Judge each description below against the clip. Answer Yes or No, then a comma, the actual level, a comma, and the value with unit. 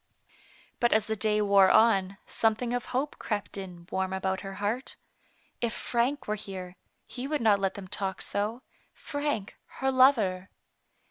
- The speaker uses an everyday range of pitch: Yes, average, 3.8 semitones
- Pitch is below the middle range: No, high, 210 Hz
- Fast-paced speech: No, average, 160 wpm